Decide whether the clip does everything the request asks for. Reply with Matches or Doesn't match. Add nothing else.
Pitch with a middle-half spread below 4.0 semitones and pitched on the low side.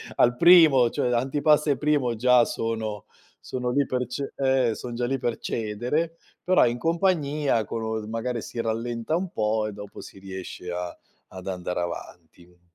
Doesn't match